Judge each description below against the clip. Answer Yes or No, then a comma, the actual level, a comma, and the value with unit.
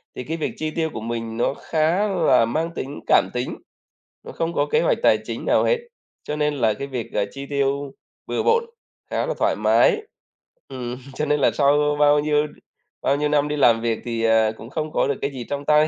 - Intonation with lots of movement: No, average, 3.8 semitones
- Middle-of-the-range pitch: Yes, medium, 145 Hz